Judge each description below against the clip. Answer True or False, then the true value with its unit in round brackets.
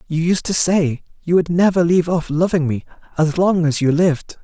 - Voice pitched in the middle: True (165 Hz)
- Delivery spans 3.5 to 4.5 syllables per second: False (5.4 syllables/s)